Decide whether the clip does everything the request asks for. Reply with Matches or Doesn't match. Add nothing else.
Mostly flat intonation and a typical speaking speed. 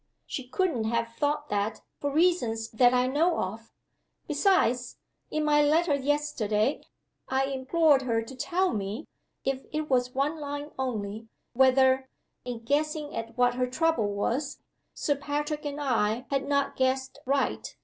Doesn't match